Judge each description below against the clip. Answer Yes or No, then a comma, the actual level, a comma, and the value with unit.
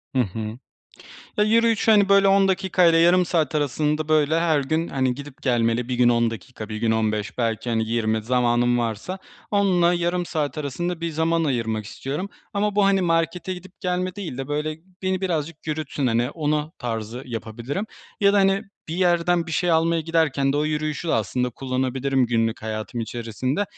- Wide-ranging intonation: Yes, wide, 6.4 semitones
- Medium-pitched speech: Yes, medium, 150 Hz